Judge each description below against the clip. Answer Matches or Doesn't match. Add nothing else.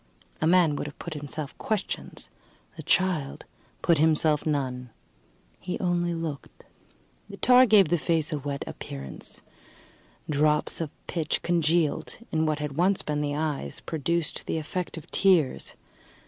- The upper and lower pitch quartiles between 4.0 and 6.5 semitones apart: Doesn't match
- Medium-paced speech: Matches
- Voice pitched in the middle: Matches